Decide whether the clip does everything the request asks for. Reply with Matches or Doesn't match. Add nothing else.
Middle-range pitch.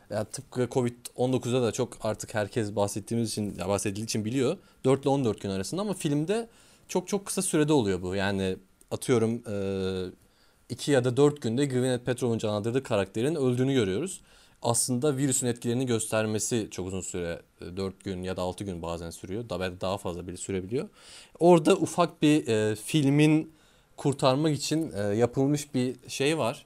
Doesn't match